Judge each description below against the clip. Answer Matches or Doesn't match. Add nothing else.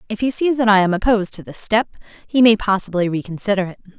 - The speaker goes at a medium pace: Doesn't match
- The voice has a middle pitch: Doesn't match